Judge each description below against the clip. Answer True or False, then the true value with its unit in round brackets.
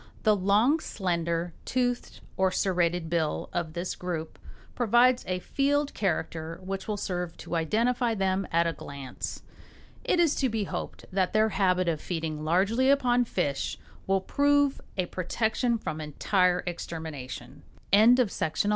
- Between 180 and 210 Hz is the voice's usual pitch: True (190 Hz)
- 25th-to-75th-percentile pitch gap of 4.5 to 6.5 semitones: True (5.6 semitones)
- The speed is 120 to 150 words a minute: True (145 wpm)